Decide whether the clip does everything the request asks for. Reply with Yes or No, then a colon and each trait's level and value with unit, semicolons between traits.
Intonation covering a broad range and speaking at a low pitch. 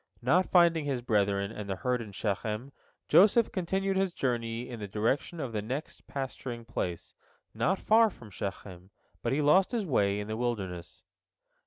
Yes: wide, 8.0 semitones; low, 120 Hz